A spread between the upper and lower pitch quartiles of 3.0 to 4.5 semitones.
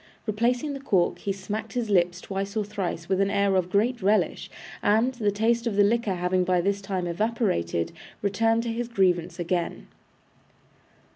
Yes: average, 3.6 semitones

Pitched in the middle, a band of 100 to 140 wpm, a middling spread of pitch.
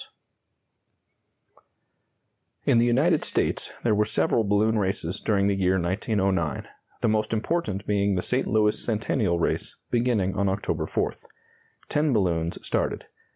No: low, 105 Hz; slow, 135 wpm; average, 3.1 semitones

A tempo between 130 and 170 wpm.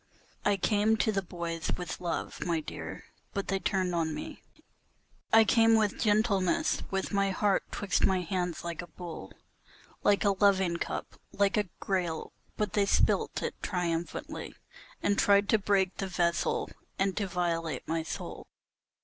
Yes: average, 160 wpm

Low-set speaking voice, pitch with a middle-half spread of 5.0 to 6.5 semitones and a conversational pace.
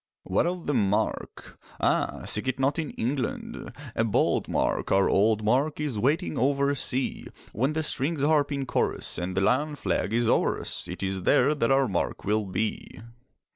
Yes: low, 130 Hz; average, 5.3 semitones; average, 180 wpm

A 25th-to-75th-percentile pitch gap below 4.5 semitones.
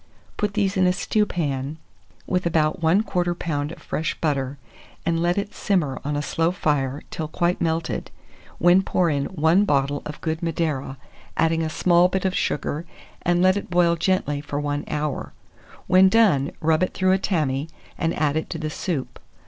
Yes: average, 3.6 semitones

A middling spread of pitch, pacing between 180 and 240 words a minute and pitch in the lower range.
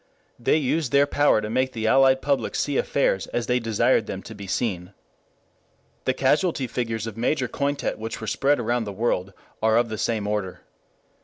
Yes: average, 3.6 semitones; average, 185 wpm; low, 120 Hz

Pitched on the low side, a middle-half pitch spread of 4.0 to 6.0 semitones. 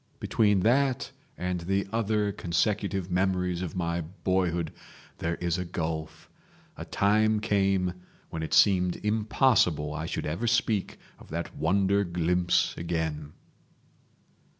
No: very low, 90 Hz; average, 3.2 semitones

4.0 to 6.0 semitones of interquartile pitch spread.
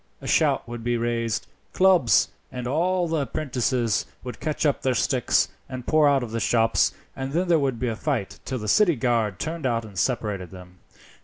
Yes: average, 4.3 semitones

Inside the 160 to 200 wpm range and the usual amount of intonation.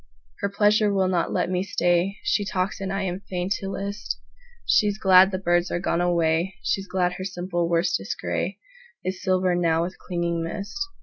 No: average, 165 wpm; narrow, 2.1 semitones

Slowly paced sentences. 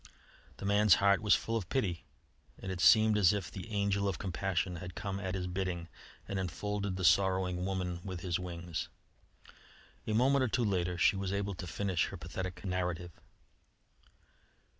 No: average, 170 wpm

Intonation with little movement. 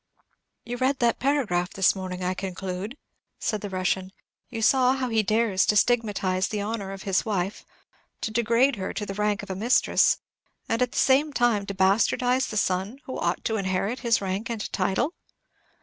No: average, 4.0 semitones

